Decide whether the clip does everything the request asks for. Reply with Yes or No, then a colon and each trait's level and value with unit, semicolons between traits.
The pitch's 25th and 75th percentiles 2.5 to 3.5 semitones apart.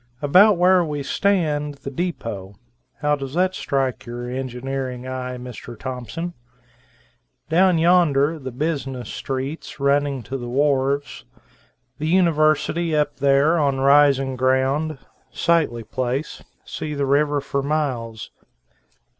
Yes: average, 3.0 semitones